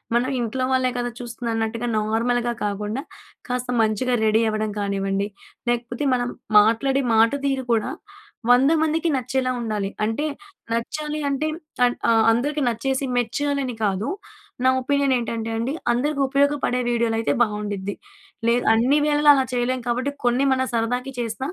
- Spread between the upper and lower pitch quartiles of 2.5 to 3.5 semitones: Yes, average, 2.9 semitones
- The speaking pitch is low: No, high, 240 Hz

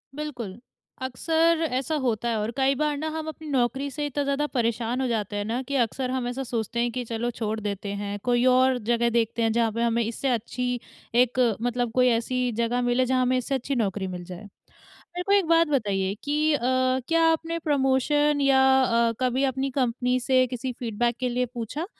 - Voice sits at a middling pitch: No, very high, 250 Hz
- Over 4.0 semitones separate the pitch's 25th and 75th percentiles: No, average, 2.9 semitones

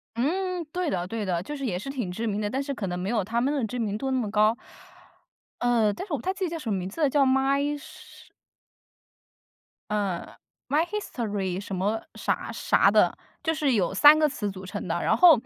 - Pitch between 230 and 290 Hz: Yes, high, 235 Hz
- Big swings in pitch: Yes, wide, 6.3 semitones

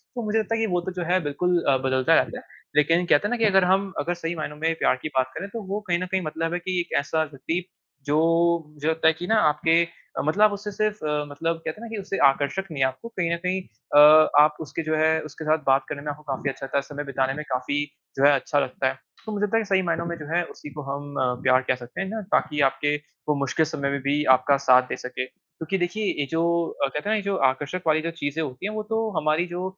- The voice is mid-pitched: Yes, medium, 155 Hz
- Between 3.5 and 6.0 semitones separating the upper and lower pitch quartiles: Yes, average, 4.4 semitones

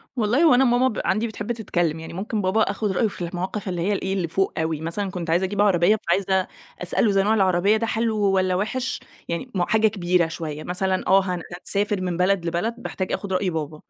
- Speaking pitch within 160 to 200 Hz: Yes, high, 190 Hz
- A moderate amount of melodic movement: Yes, average, 3.3 semitones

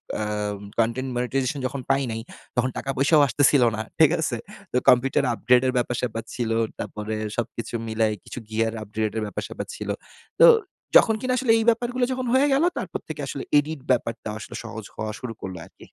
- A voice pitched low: Yes, low, 125 Hz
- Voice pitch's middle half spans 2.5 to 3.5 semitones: No, average, 4.3 semitones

